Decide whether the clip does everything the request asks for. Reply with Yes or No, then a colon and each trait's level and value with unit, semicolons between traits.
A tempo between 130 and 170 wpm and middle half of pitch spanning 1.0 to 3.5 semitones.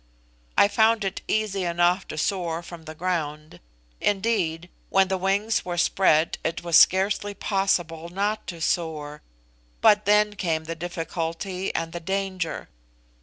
Yes: average, 140 wpm; average, 3.1 semitones